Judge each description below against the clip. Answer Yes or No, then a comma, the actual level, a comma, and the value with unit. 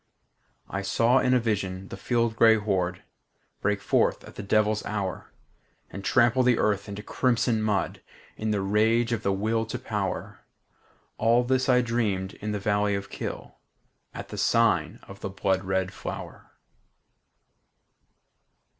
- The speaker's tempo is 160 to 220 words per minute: No, average, 150 wpm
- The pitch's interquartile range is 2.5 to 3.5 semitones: Yes, average, 3.0 semitones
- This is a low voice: Yes, low, 105 Hz